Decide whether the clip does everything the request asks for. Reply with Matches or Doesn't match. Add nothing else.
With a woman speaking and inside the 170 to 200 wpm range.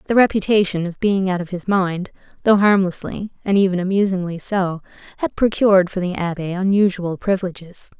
Doesn't match